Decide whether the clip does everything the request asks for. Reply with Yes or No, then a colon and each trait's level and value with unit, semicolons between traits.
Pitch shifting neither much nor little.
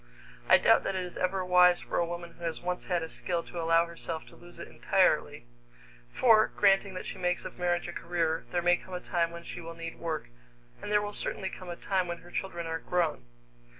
No: narrow, 1.4 semitones